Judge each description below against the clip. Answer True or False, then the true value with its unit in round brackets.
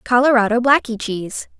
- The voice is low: False (235 Hz)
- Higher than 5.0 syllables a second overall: True (5.6 syllables/s)